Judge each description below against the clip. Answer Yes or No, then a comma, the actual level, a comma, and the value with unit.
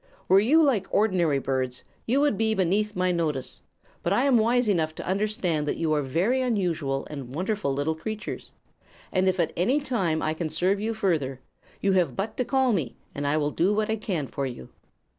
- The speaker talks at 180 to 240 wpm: Yes, fast, 205 wpm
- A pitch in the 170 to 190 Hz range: Yes, medium, 185 Hz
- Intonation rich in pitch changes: Yes, wide, 5.9 semitones